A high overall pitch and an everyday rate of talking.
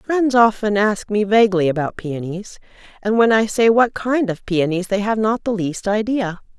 Yes: high, 210 Hz; average, 190 wpm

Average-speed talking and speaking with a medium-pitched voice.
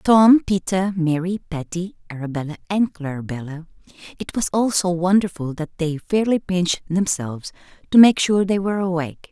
Yes: average, 155 wpm; medium, 180 Hz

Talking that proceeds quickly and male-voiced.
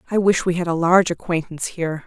No: fast, 235 wpm; female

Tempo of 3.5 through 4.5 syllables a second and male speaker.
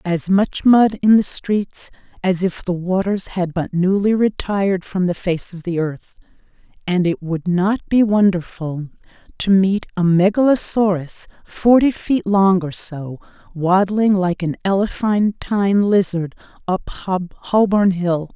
No: 4.1 syllables/s; female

